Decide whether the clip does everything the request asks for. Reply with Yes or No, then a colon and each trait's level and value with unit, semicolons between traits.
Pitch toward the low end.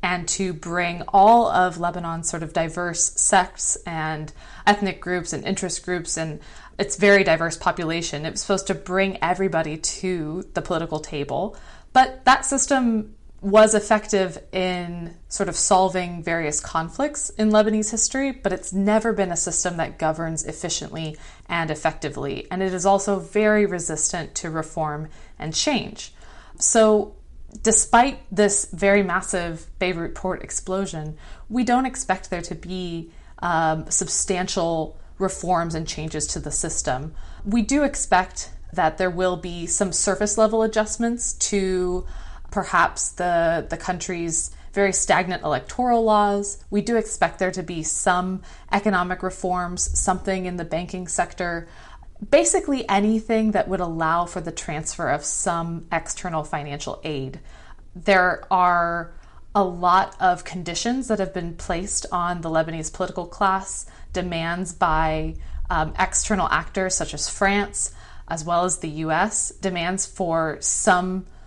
No: medium, 180 Hz